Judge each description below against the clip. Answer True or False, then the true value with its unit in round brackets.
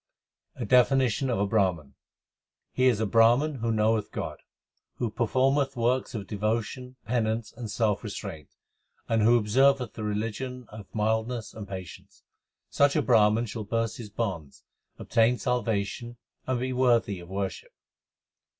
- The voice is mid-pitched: False (115 Hz)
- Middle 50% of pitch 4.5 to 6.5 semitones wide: False (3.0 semitones)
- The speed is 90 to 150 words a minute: True (140 wpm)